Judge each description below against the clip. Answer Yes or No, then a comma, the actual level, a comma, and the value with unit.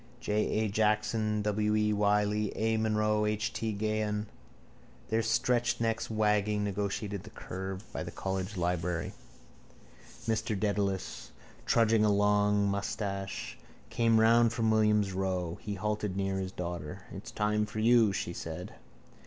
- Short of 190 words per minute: Yes, average, 140 wpm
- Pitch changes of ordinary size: No, narrow, 1.8 semitones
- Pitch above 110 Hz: No, low, 105 Hz